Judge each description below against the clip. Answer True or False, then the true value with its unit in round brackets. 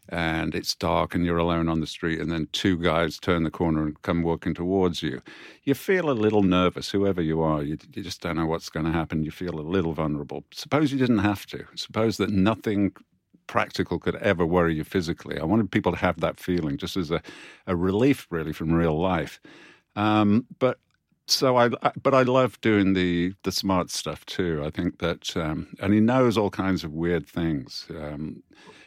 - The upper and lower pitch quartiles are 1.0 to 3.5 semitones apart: False (4.0 semitones)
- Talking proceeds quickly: True (210 wpm)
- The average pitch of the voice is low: True (90 Hz)